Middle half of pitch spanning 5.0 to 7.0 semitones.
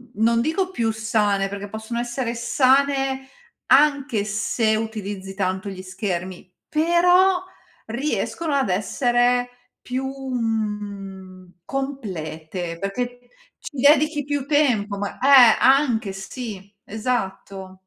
Yes: average, 5.3 semitones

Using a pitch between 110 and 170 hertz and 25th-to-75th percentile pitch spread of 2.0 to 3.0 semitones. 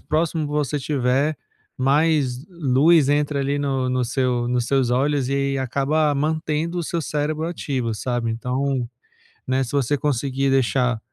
Yes: medium, 140 Hz; average, 2.7 semitones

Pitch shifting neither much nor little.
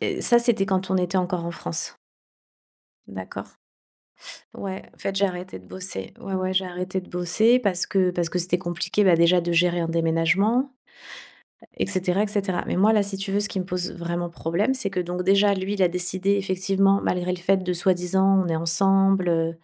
No: narrow, 1.9 semitones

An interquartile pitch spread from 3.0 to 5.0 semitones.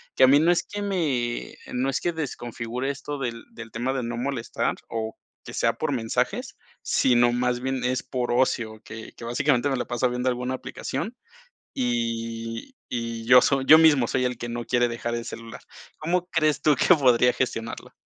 No: narrow, 2.5 semitones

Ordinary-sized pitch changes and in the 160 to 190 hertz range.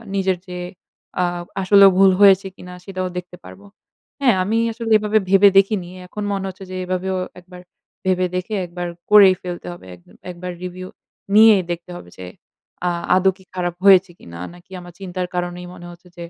No: narrow, 1.7 semitones; medium, 185 Hz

